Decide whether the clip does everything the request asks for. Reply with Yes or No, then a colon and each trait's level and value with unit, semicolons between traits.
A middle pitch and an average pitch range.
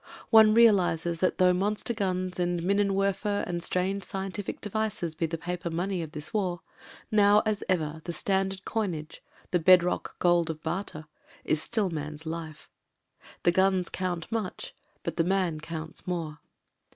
Yes: medium, 180 Hz; average, 3.0 semitones